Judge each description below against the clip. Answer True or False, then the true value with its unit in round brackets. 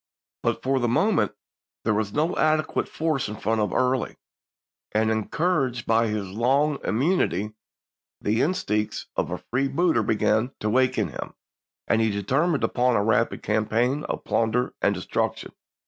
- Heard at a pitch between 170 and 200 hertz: False (120 Hz)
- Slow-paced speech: False (155 wpm)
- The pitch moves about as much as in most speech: True (4.1 semitones)